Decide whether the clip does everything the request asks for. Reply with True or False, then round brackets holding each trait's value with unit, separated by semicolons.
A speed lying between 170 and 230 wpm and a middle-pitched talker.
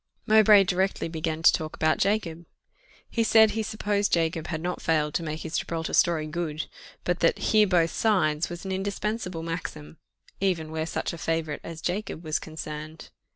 True (175 wpm; 165 Hz)